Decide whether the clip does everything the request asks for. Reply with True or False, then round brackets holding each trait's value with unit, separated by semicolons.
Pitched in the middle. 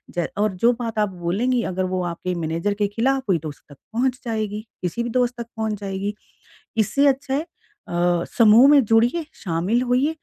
False (215 Hz)